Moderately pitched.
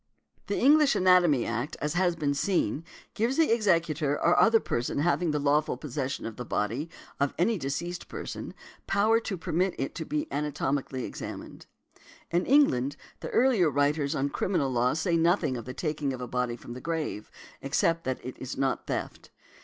Yes: medium, 150 Hz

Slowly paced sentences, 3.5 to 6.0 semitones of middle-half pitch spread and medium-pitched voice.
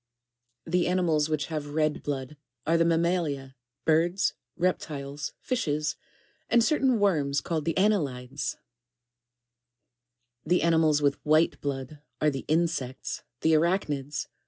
No: slow, 120 wpm; average, 2.9 semitones; medium, 155 Hz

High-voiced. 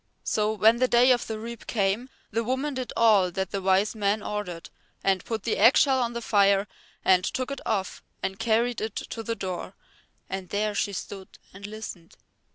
Yes: high, 215 Hz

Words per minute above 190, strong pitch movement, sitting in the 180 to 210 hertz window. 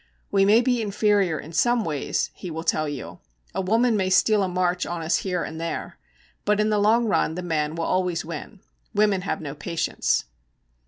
No: average, 200 wpm; average, 4.2 semitones; medium, 185 Hz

